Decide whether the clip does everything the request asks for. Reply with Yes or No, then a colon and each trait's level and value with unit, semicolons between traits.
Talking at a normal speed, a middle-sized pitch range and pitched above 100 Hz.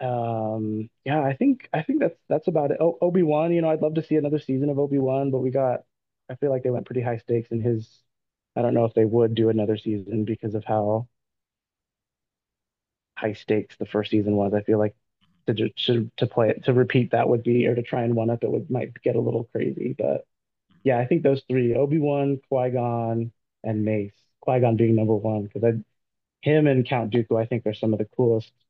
No: fast, 230 wpm; average, 3.2 semitones; low, 120 Hz